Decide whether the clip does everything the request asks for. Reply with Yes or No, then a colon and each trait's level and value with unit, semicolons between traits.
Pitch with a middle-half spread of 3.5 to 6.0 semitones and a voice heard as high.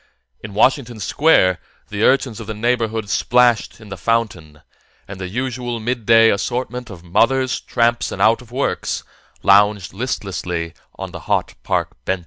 No: average, 3.8 semitones; low, 115 Hz